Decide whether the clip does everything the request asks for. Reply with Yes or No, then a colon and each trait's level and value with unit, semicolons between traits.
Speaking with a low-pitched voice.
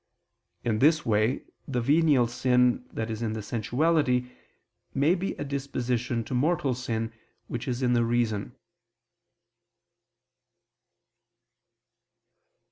Yes: low, 125 Hz